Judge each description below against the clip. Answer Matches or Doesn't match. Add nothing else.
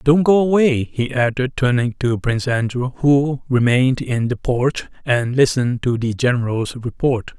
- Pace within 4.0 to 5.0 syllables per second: Matches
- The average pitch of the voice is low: Matches